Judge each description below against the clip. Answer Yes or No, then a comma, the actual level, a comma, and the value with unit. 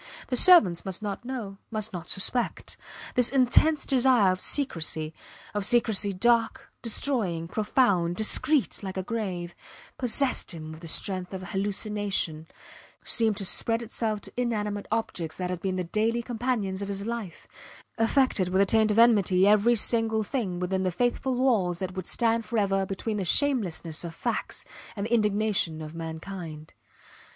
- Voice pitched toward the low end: No, high, 205 Hz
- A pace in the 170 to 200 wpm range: No, average, 160 wpm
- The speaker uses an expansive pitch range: No, average, 4.1 semitones